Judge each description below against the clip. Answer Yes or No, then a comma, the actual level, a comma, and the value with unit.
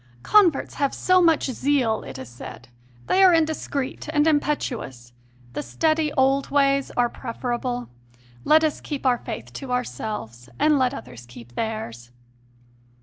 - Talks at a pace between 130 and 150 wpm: Yes, average, 145 wpm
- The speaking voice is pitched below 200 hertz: No, very high, 260 Hz